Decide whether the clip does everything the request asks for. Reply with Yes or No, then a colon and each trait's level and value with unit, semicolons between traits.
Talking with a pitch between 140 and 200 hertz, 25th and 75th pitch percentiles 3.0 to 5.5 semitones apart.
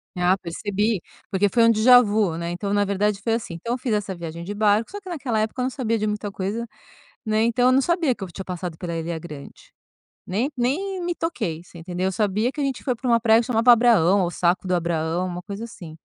No: high, 210 Hz; average, 4.9 semitones